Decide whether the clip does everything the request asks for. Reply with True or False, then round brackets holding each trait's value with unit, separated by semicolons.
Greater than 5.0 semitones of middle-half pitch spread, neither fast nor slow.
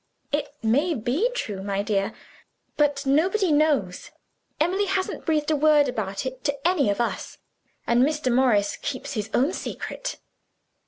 True (5.5 semitones; 150 wpm)